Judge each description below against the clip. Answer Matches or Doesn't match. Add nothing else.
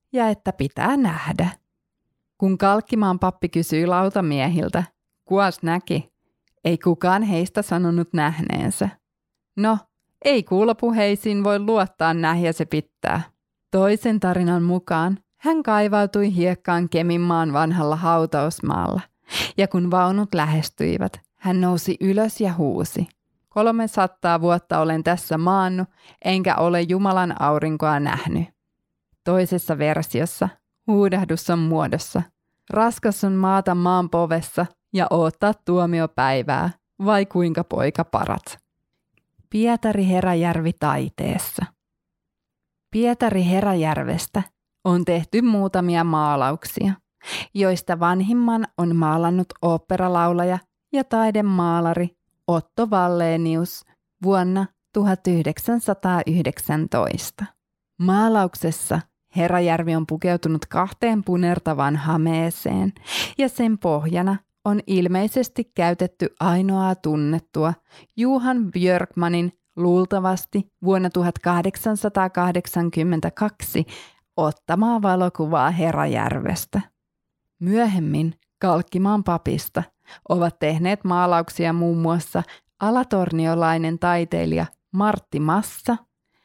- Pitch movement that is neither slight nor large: Matches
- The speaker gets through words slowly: Matches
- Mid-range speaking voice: Matches